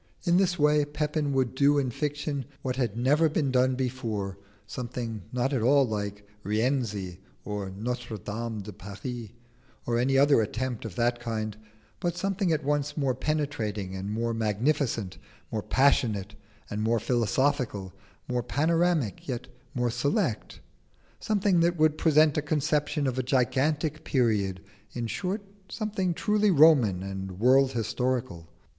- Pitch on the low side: Yes, low, 125 Hz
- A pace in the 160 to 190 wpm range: No, average, 145 wpm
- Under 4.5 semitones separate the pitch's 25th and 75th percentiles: No, average, 5.2 semitones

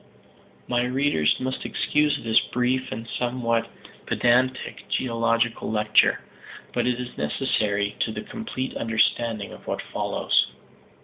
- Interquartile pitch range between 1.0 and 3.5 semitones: Yes, narrow, 2.5 semitones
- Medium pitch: No, low, 120 Hz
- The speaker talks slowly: Yes, slow, 120 wpm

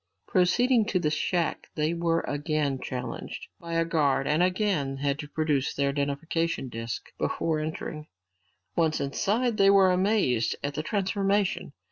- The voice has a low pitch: No, medium, 160 Hz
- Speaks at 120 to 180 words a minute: Yes, average, 145 wpm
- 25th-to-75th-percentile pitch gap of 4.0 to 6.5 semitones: Yes, average, 4.7 semitones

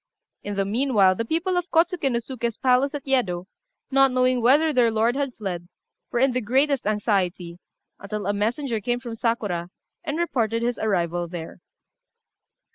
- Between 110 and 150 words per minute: No, average, 165 wpm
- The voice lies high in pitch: Yes, high, 235 Hz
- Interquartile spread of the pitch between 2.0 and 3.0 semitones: No, average, 4.9 semitones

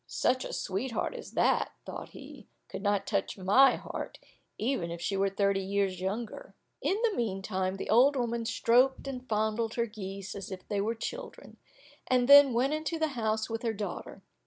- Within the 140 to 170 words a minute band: No, average, 185 wpm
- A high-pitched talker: Yes, high, 220 Hz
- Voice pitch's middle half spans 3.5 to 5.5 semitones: Yes, average, 4.4 semitones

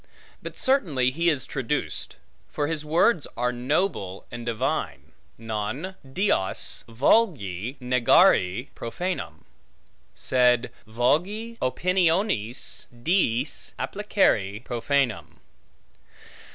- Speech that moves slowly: Yes, slow, 85 wpm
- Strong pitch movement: Yes, wide, 7.0 semitones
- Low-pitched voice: Yes, low, 130 Hz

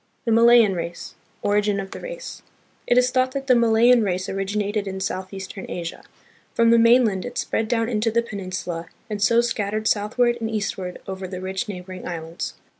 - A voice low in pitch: No, high, 210 Hz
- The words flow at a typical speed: Yes, average, 185 wpm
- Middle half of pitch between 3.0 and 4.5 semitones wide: Yes, average, 3.6 semitones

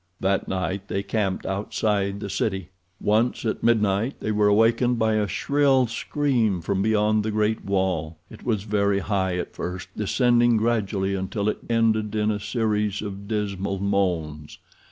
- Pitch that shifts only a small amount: Yes, narrow, 2.2 semitones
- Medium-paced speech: Yes, average, 155 wpm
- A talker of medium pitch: No, low, 105 Hz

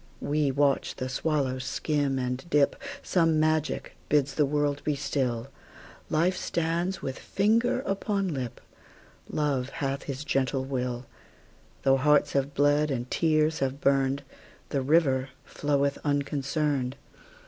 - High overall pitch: No, medium, 140 Hz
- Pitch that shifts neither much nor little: No, narrow, 2.3 semitones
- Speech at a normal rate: No, slow, 110 wpm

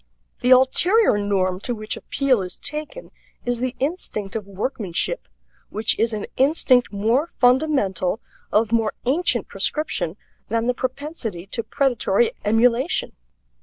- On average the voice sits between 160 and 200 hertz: No, high, 245 Hz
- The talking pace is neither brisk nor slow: No, slow, 130 wpm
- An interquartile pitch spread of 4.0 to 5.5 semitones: Yes, average, 5.0 semitones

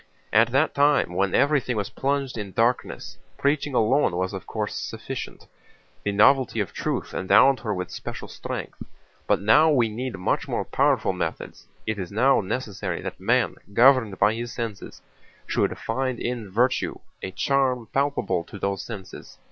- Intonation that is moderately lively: Yes, average, 4.8 semitones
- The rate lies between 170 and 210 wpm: No, average, 160 wpm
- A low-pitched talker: Yes, low, 115 Hz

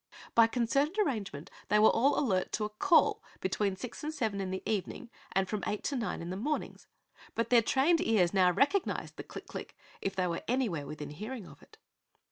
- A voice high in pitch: Yes, high, 215 Hz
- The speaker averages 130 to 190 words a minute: No, fast, 205 wpm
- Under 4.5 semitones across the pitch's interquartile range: No, wide, 5.6 semitones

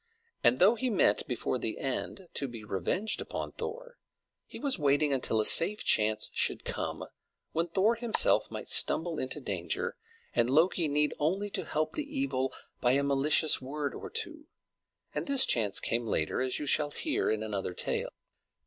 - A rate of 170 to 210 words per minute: Yes, average, 175 wpm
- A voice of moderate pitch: Yes, medium, 150 Hz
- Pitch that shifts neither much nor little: No, wide, 9.0 semitones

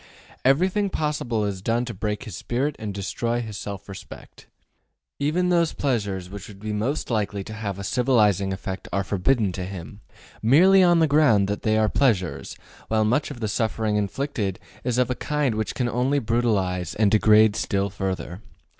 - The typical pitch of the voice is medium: No, low, 110 Hz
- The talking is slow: No, average, 180 wpm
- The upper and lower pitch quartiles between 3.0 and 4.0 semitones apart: No, average, 4.4 semitones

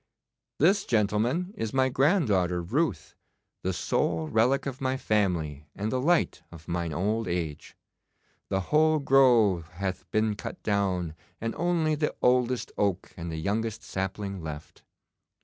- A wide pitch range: Yes, wide, 6.8 semitones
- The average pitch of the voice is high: No, low, 105 Hz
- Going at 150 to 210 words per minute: No, average, 140 wpm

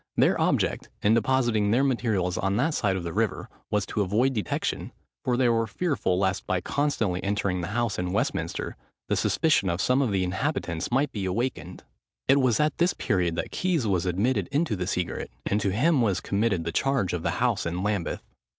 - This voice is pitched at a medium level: No, low, 105 Hz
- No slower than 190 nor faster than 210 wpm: Yes, average, 200 wpm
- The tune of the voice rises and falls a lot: Yes, wide, 5.7 semitones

